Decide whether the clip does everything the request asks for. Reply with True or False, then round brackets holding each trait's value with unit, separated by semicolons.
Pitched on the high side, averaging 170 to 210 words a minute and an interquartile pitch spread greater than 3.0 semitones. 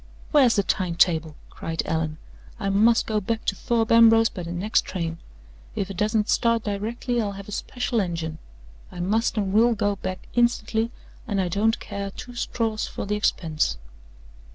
True (205 Hz; 175 wpm; 3.7 semitones)